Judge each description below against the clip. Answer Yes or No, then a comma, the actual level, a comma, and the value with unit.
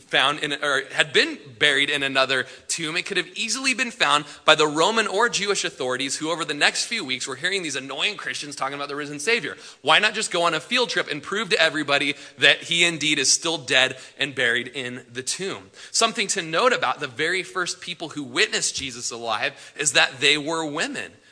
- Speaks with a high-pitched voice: No, medium, 155 Hz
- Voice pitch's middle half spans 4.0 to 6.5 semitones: Yes, average, 4.7 semitones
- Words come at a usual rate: No, fast, 215 wpm